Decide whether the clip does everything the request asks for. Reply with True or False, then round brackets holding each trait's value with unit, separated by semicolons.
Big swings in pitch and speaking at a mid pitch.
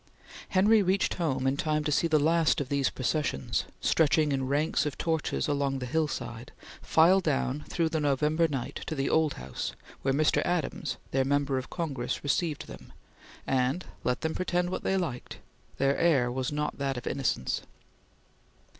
False (3.2 semitones; 145 Hz)